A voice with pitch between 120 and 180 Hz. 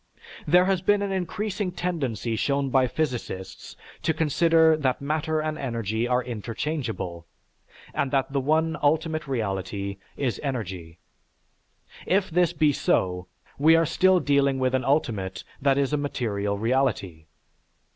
Yes: medium, 140 Hz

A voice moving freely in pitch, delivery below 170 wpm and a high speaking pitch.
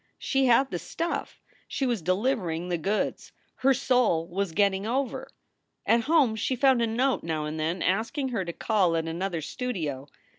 No: wide, 6.8 semitones; average, 180 wpm; high, 205 Hz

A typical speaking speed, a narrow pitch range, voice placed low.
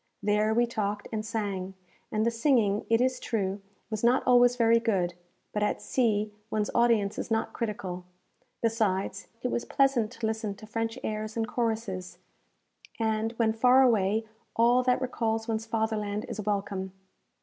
No: average, 160 wpm; narrow, 2.0 semitones; high, 220 Hz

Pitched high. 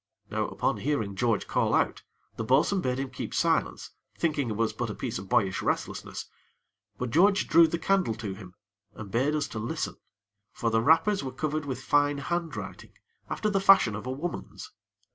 No: low, 130 Hz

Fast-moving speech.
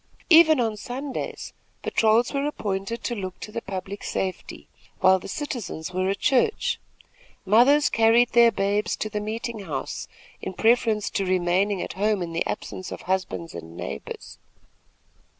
No: average, 150 wpm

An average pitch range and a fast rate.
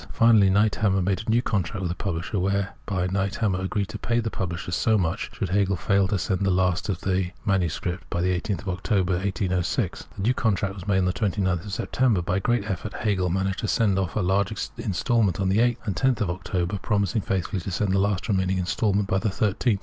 No: narrow, 2.2 semitones; fast, 215 wpm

